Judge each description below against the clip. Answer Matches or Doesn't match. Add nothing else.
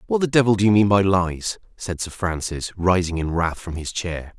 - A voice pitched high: Doesn't match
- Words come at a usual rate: Doesn't match